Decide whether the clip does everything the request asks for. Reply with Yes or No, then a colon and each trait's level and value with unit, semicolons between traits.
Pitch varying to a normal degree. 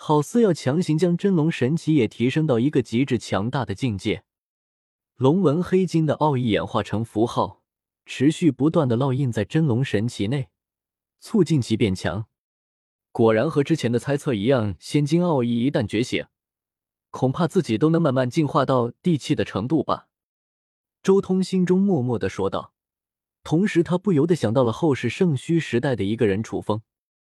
No: wide, 6.7 semitones